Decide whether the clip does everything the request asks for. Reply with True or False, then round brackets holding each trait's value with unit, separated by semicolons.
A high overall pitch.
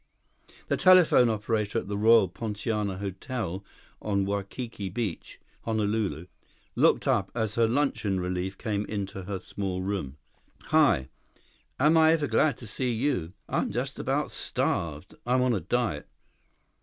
False (105 Hz)